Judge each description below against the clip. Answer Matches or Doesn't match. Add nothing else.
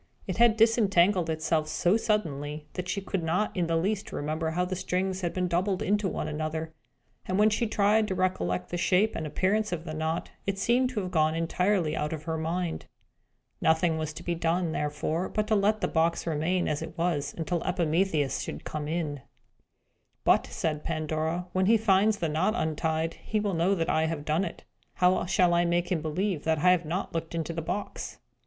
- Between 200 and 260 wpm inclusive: Matches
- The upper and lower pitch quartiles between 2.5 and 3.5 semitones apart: Matches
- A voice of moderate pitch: Matches